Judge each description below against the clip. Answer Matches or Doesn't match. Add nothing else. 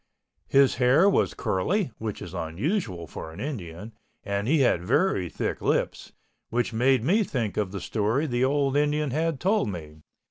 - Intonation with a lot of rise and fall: Matches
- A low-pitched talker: Matches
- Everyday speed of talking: Matches